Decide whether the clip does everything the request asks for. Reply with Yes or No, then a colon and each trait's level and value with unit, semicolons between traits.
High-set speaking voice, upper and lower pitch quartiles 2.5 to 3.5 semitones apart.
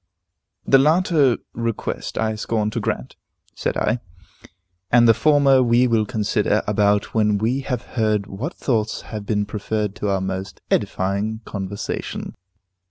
No: low, 110 Hz; average, 3.0 semitones